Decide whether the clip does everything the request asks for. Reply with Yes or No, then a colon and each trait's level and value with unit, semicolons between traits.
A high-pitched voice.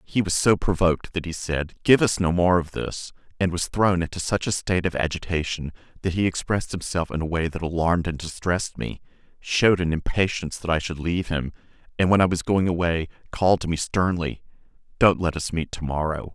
No: very low, 85 Hz